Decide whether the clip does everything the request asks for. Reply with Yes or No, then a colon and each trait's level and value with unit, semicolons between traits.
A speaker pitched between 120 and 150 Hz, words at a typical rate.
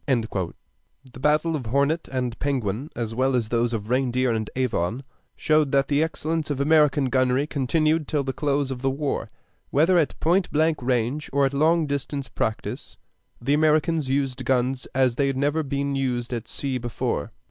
Yes: low, 135 Hz; average, 180 wpm